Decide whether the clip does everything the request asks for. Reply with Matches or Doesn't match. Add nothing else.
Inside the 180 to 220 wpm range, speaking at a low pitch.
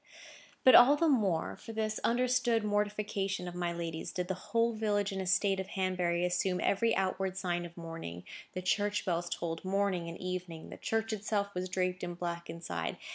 Doesn't match